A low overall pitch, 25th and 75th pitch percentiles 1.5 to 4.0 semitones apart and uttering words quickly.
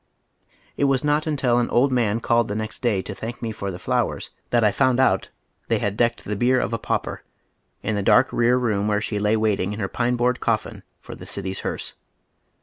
Yes: low, 115 Hz; average, 3.0 semitones; fast, 225 wpm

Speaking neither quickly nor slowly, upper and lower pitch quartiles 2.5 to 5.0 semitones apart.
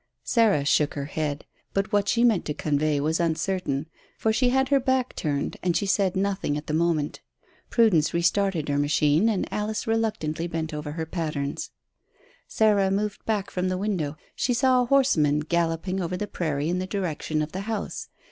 No: average, 185 wpm; wide, 5.4 semitones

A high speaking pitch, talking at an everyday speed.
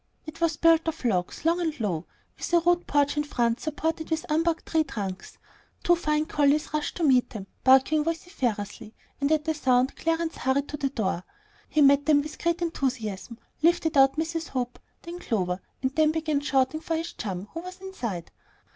Yes: very high, 300 Hz; average, 190 wpm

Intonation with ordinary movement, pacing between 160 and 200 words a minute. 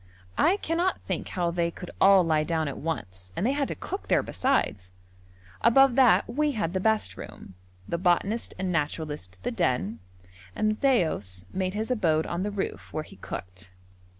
No: wide, 7.1 semitones; average, 180 wpm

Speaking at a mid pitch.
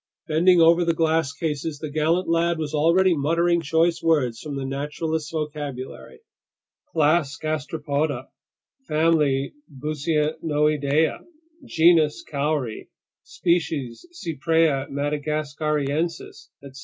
Yes: medium, 155 Hz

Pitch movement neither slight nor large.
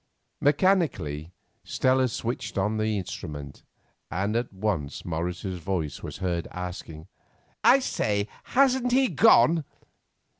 No: wide, 7.2 semitones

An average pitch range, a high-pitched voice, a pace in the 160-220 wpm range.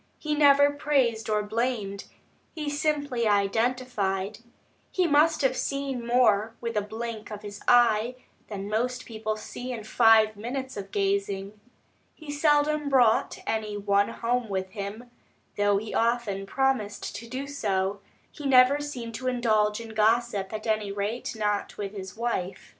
No: average, 3.8 semitones; high, 225 Hz; average, 150 wpm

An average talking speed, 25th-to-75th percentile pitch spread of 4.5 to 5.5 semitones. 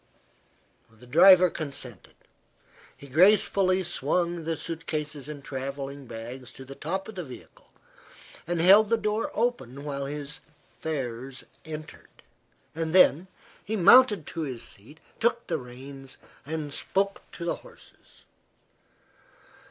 No: slow, 125 wpm; average, 5.1 semitones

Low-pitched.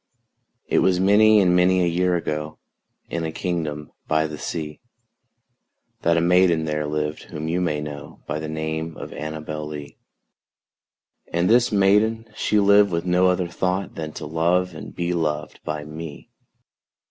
Yes: very low, 85 Hz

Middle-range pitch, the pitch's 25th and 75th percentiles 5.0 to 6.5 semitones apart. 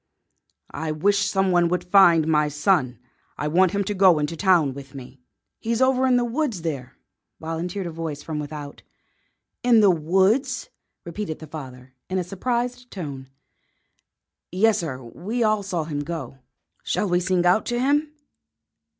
Yes: medium, 175 Hz; wide, 5.5 semitones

